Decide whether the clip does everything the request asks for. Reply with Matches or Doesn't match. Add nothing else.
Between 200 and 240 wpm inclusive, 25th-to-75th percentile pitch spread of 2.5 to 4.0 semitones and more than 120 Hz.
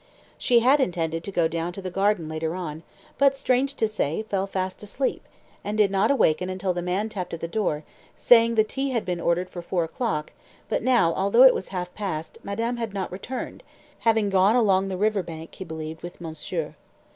Doesn't match